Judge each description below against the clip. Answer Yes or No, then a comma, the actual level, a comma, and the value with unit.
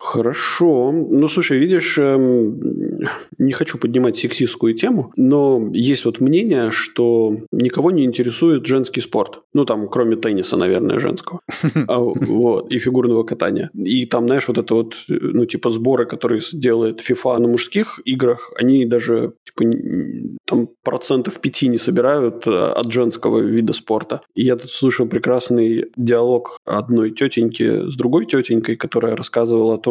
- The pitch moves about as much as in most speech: No, narrow, 2.2 semitones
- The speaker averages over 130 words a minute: Yes, average, 145 wpm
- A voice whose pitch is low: Yes, low, 120 Hz